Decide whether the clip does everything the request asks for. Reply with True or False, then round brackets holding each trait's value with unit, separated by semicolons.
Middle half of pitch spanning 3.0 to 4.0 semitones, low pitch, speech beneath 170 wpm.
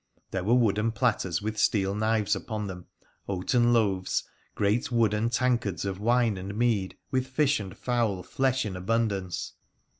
True (3.5 semitones; 110 Hz; 150 wpm)